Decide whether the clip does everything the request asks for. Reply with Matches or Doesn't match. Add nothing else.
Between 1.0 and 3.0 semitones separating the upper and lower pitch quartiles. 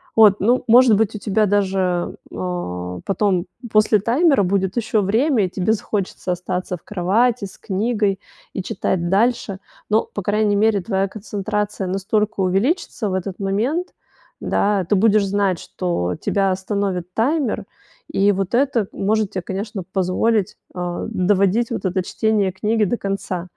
Matches